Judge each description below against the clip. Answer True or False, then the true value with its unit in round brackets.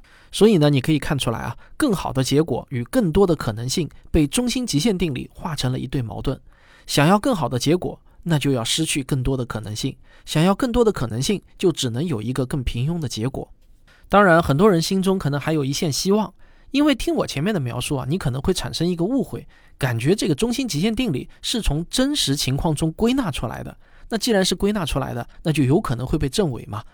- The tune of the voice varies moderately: False (6.5 semitones)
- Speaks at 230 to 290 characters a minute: False (335 characters per minute)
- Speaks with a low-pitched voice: False (155 Hz)